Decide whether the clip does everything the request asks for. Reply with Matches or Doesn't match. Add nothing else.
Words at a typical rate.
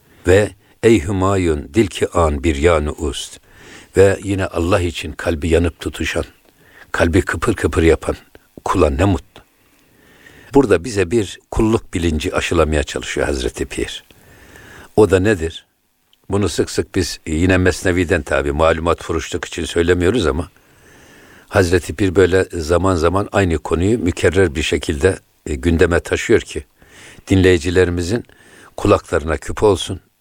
Matches